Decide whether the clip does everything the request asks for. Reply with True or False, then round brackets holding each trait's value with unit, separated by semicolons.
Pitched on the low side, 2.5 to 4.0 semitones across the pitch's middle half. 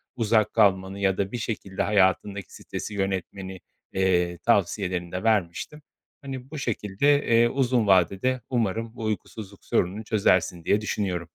True (100 Hz; 3.4 semitones)